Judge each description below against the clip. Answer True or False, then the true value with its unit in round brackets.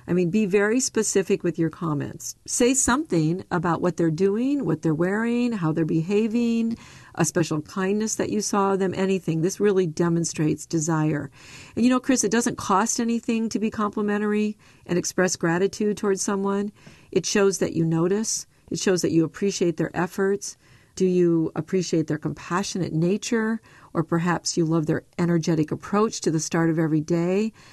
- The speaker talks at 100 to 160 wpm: False (170 wpm)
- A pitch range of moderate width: True (4.1 semitones)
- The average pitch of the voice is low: False (185 Hz)